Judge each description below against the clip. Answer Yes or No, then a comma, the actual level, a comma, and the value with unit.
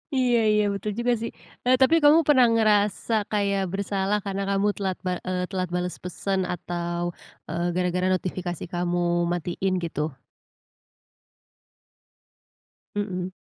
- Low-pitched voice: No, high, 190 Hz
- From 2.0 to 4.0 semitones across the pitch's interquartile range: Yes, average, 2.8 semitones